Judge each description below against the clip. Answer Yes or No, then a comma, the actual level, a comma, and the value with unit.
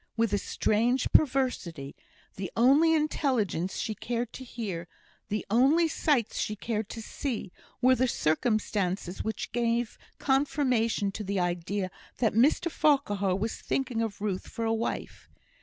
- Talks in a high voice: Yes, high, 225 Hz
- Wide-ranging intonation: No, average, 4.3 semitones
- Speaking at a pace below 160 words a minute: Yes, average, 140 wpm